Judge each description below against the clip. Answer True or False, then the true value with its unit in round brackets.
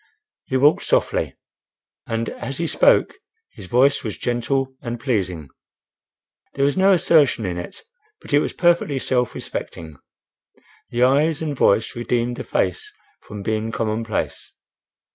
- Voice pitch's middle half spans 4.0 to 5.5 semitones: True (4.4 semitones)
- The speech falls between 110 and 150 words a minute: True (140 wpm)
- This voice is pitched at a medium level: False (125 Hz)